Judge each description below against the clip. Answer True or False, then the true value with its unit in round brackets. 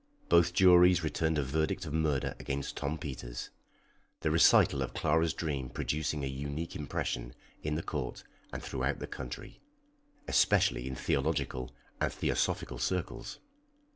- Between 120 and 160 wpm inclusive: True (140 wpm)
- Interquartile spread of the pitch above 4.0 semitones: False (3.4 semitones)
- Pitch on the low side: True (75 Hz)